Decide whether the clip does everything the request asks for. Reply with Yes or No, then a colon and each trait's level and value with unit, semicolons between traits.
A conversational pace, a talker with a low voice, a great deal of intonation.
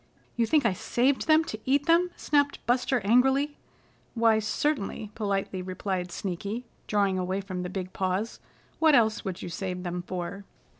No: average, 160 wpm; high, 210 Hz; wide, 5.8 semitones